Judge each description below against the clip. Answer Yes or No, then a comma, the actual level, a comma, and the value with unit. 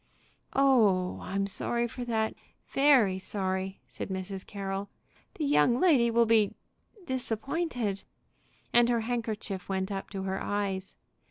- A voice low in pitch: No, high, 210 Hz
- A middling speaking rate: No, slow, 125 wpm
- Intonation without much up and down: No, average, 3.8 semitones